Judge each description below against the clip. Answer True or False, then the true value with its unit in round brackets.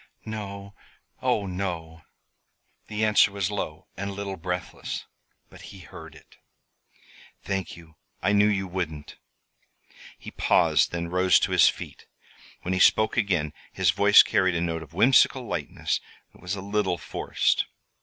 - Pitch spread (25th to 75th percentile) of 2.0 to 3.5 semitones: True (2.9 semitones)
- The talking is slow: False (150 wpm)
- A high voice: False (95 Hz)